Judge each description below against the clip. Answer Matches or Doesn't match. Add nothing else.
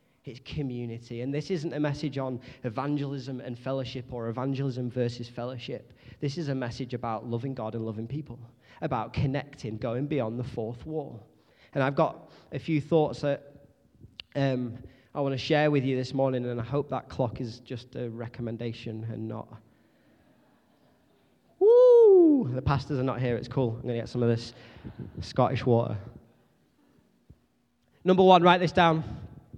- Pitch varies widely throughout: Doesn't match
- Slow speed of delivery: Doesn't match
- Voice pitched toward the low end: Matches